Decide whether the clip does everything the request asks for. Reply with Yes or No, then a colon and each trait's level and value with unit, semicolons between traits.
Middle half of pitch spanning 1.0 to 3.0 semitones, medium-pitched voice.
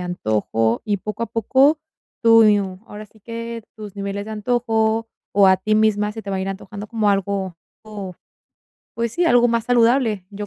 No: narrow, 2.6 semitones; high, 215 Hz